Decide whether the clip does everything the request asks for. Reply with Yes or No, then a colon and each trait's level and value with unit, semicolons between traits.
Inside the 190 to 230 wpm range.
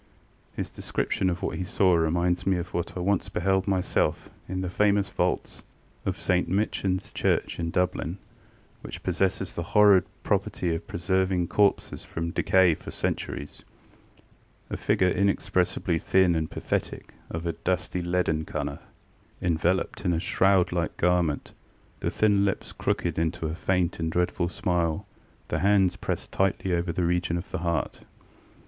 No: average, 155 wpm